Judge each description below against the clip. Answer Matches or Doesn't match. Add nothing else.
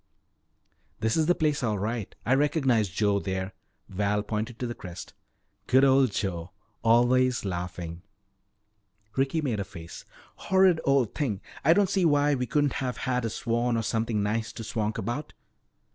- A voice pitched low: Matches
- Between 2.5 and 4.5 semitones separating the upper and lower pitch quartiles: Doesn't match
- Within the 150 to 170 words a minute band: Matches